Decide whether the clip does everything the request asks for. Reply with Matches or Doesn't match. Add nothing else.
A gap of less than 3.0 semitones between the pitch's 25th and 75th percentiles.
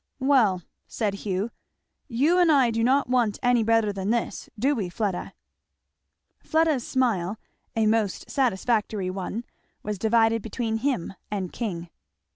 Doesn't match